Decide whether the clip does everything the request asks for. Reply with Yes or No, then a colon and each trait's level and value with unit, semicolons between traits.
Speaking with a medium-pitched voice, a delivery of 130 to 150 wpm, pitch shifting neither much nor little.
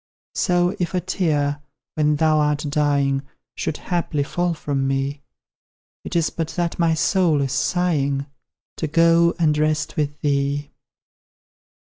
Yes: medium, 150 Hz; slow, 135 wpm; average, 3.0 semitones